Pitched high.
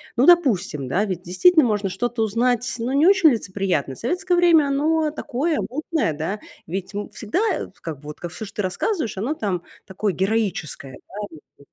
Yes: high, 215 Hz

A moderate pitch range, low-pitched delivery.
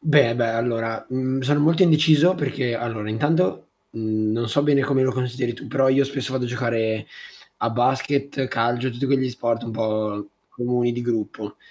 Yes: average, 3.2 semitones; low, 125 Hz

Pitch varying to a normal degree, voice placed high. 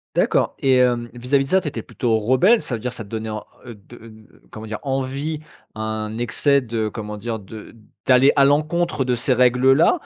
No: average, 3.8 semitones; low, 125 Hz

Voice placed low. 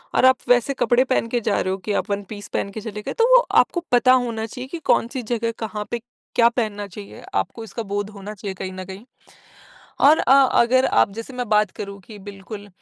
No: high, 220 Hz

